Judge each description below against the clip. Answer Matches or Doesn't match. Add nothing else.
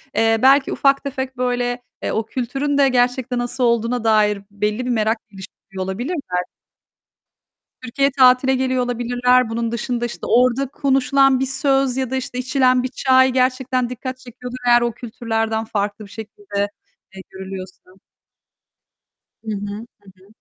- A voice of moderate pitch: Doesn't match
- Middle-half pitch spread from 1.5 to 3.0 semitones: Matches